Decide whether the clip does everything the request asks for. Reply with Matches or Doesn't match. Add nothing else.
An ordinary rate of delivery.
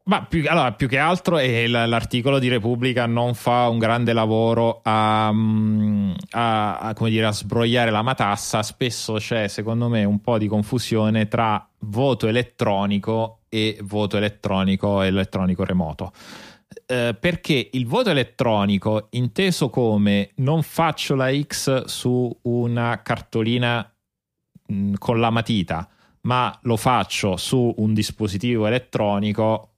Matches